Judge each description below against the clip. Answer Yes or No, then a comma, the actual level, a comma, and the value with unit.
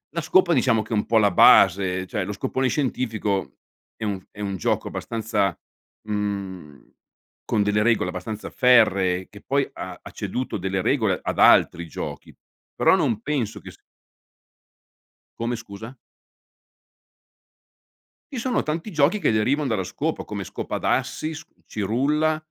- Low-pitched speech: Yes, low, 110 Hz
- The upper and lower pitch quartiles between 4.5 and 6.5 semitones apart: Yes, average, 5.1 semitones